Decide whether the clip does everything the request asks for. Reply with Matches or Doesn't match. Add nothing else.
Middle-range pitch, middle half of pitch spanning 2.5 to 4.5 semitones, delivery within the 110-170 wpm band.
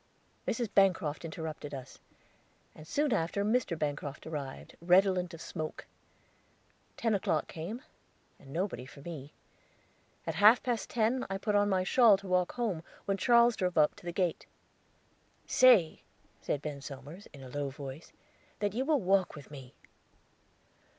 Doesn't match